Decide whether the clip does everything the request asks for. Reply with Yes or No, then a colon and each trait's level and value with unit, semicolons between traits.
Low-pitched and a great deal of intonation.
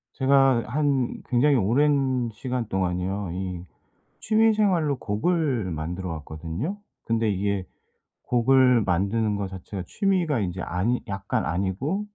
Yes: low, 115 Hz; wide, 6.5 semitones